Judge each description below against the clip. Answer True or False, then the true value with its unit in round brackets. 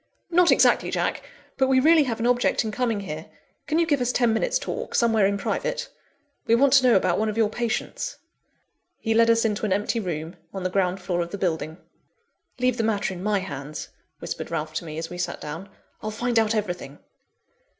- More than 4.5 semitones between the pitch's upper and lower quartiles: True (5.2 semitones)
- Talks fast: True (210 wpm)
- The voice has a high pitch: True (215 Hz)